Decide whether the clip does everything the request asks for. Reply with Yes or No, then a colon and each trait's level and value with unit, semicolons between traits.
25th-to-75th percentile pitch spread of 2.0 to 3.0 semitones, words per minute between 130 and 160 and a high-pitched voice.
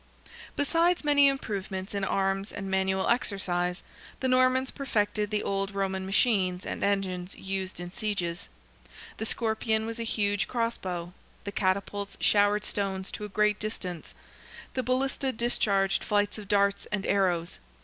Yes: narrow, 2.5 semitones; average, 145 wpm; high, 200 Hz